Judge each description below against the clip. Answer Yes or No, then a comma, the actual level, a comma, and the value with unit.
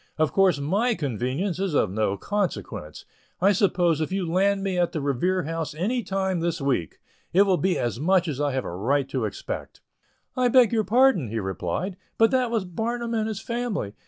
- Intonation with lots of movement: Yes, wide, 6.2 semitones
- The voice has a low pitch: No, medium, 180 Hz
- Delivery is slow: No, average, 200 wpm